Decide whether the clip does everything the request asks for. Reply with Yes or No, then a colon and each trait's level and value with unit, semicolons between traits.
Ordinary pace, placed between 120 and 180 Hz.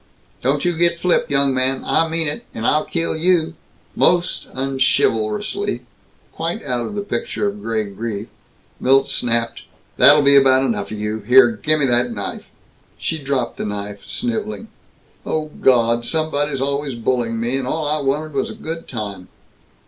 Yes: average, 165 wpm; low, 135 Hz